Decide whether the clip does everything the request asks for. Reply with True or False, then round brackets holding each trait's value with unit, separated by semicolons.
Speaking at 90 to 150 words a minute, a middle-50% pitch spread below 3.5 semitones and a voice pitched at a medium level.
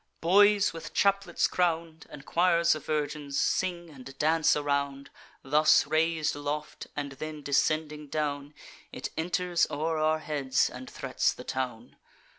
True (135 wpm; 2.7 semitones; 155 Hz)